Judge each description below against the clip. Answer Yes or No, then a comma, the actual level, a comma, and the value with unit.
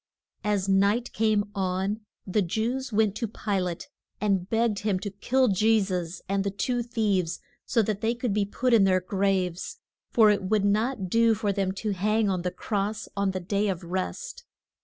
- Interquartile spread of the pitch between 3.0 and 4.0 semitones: No, narrow, 2.6 semitones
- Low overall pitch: No, high, 205 Hz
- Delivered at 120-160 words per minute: No, average, 195 wpm